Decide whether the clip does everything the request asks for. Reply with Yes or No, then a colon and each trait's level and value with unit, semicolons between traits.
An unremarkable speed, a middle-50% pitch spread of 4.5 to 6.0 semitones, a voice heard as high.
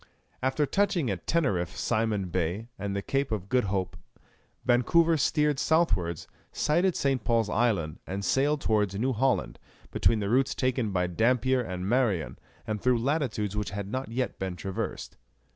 No: average, 160 wpm; average, 5.2 semitones; low, 115 Hz